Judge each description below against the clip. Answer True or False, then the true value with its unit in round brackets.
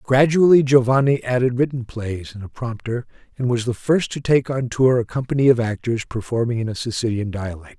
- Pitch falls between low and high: False (120 Hz)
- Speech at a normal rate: True (195 wpm)